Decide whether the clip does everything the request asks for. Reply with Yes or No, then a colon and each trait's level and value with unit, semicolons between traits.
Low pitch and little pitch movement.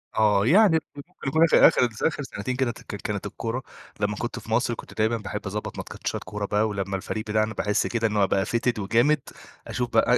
No: low, 110 Hz; average, 3.3 semitones